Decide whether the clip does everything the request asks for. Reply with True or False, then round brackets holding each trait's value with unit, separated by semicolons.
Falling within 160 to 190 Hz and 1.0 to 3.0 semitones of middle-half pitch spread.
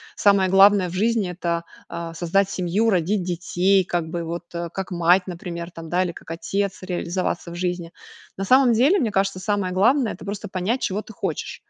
True (185 Hz; 2.7 semitones)